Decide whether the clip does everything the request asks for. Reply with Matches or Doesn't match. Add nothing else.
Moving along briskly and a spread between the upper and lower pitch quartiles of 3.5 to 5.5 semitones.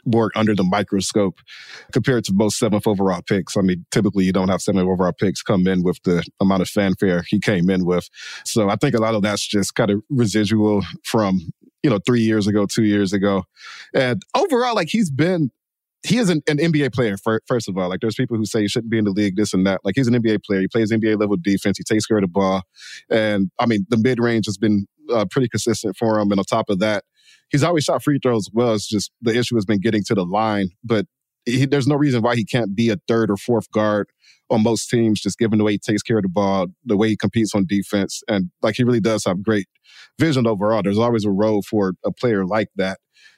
Doesn't match